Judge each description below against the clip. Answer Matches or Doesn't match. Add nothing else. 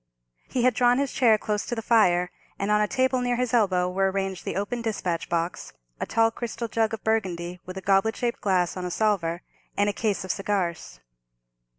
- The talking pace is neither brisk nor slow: Doesn't match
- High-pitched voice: Matches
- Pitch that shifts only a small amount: Doesn't match